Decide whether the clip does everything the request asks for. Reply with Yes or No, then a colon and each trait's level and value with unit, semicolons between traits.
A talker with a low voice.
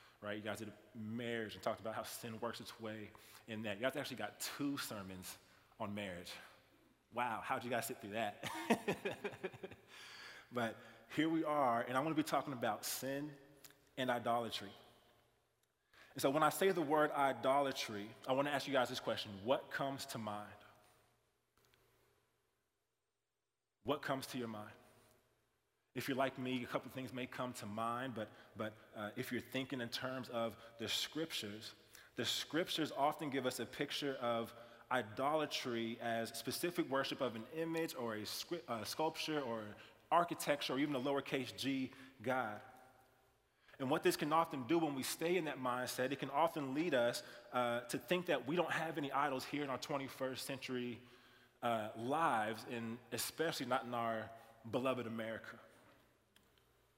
Yes: low, 125 Hz